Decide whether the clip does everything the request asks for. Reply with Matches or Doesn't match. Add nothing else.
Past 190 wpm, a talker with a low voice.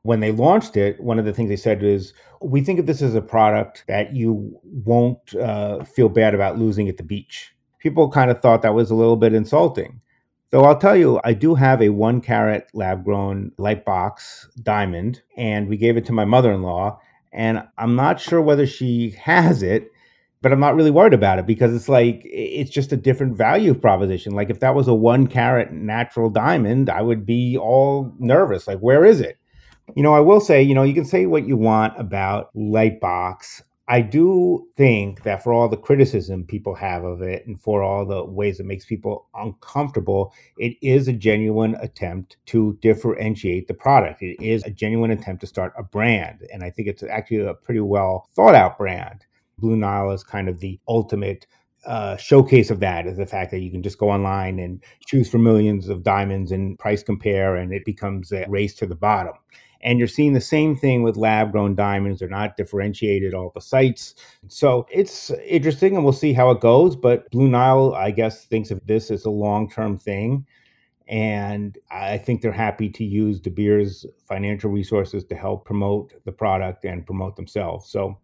Matches